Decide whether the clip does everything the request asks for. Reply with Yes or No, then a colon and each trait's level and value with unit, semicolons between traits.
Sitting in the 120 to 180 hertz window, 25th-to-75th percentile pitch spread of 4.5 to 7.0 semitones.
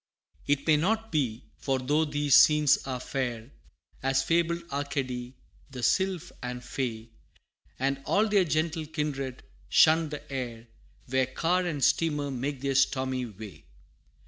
No: medium, 140 Hz; average, 3.5 semitones